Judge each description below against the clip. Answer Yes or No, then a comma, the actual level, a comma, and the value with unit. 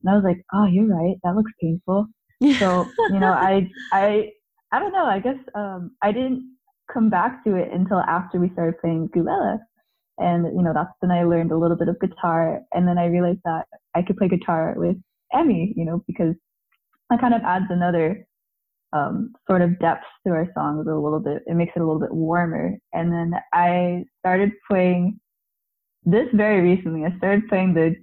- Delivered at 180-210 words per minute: Yes, average, 200 wpm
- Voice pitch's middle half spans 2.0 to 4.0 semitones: Yes, average, 3.7 semitones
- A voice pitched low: No, medium, 185 Hz